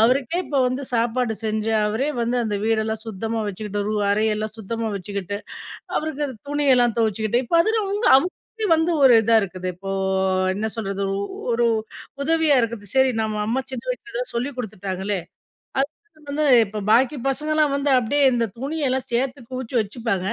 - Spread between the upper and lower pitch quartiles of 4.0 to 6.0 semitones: Yes, average, 4.5 semitones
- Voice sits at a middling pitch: No, high, 235 Hz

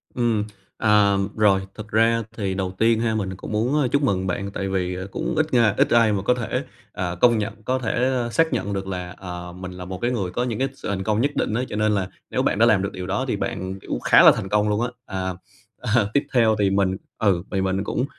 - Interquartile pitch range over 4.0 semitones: No, average, 3.4 semitones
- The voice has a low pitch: Yes, low, 105 Hz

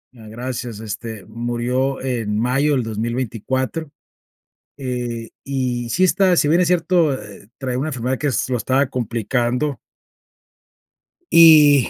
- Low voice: Yes, low, 125 Hz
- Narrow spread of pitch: No, average, 3.4 semitones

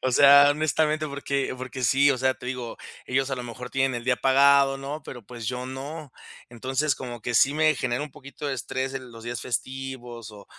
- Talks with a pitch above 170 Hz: No, low, 130 Hz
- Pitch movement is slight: Yes, narrow, 2.2 semitones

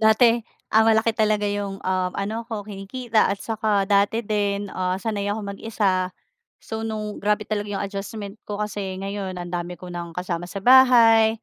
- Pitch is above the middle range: Yes, high, 205 Hz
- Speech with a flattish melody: Yes, narrow, 2.2 semitones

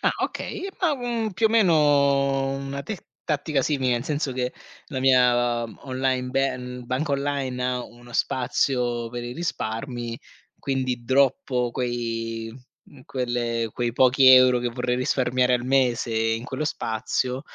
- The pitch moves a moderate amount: No, narrow, 2.2 semitones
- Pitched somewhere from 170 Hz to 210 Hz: No, low, 130 Hz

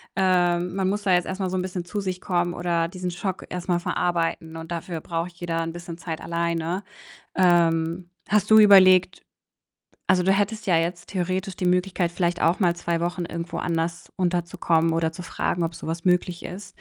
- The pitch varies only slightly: Yes, narrow, 1.6 semitones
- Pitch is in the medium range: Yes, medium, 175 Hz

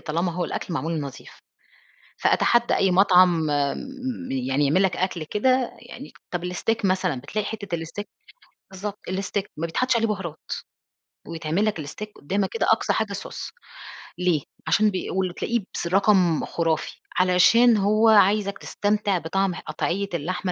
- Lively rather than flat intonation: No, average, 3.8 semitones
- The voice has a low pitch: No, high, 190 Hz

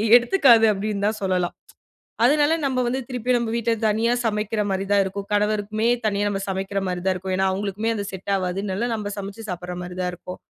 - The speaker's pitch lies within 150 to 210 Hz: Yes, high, 205 Hz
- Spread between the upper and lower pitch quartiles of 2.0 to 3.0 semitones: Yes, average, 2.7 semitones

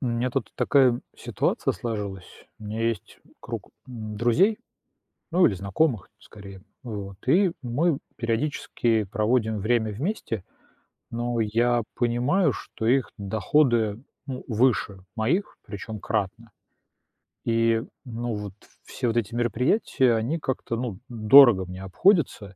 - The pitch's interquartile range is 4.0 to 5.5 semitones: No, average, 3.1 semitones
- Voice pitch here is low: Yes, low, 115 Hz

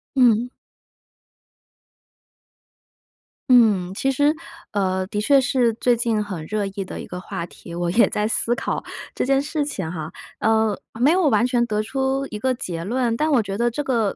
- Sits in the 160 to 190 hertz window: No, high, 225 Hz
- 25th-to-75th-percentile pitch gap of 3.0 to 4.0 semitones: No, average, 4.8 semitones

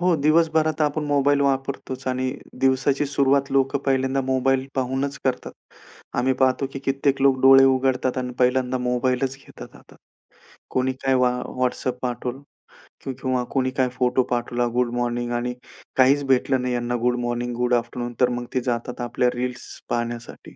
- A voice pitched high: No, low, 130 Hz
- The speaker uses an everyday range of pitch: No, narrow, 1.6 semitones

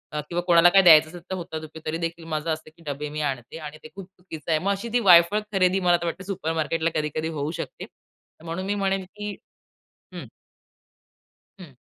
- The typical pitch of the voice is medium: Yes, medium, 170 Hz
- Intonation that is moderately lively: Yes, average, 3.1 semitones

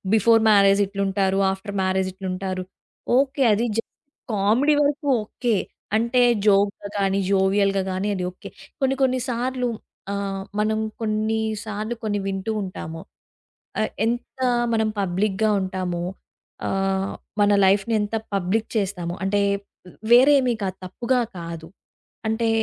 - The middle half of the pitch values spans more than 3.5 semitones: No, average, 2.8 semitones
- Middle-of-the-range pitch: No, high, 205 Hz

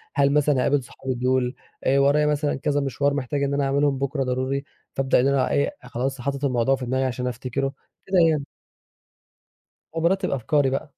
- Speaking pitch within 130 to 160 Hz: Yes, low, 135 Hz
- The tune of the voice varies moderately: No, narrow, 1.7 semitones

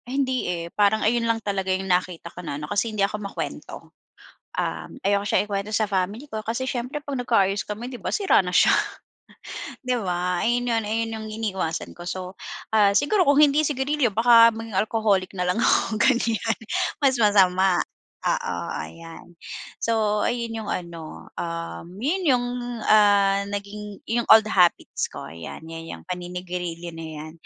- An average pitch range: Yes, average, 4.2 semitones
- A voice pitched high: Yes, high, 210 Hz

